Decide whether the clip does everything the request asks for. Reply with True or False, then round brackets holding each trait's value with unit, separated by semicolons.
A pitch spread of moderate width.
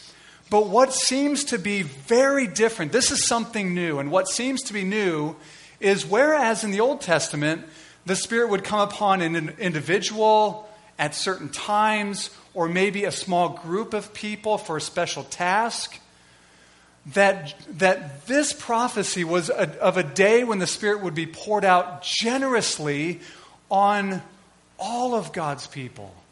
True (4.8 semitones)